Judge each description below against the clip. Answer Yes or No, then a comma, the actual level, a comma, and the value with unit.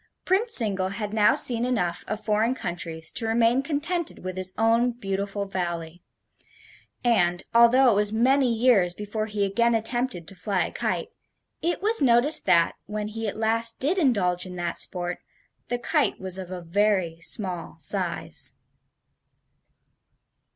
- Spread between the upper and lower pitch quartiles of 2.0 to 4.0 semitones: No, average, 4.5 semitones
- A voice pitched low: No, high, 210 Hz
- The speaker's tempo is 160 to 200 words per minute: No, average, 150 wpm